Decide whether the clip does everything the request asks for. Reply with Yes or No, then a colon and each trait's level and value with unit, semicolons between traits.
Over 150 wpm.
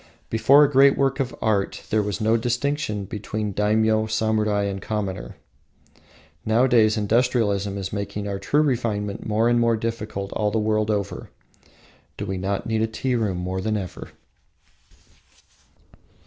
No: average, 145 wpm